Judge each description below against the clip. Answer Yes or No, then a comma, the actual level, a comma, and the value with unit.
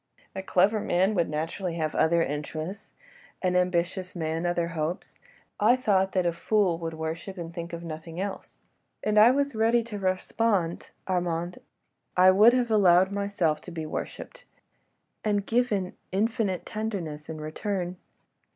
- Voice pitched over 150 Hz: Yes, medium, 185 Hz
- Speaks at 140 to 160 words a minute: Yes, average, 150 wpm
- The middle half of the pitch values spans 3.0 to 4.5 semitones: Yes, average, 3.7 semitones